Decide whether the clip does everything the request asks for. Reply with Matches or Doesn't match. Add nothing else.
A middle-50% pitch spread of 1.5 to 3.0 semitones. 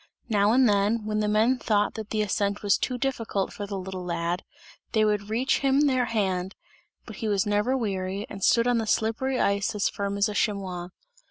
Matches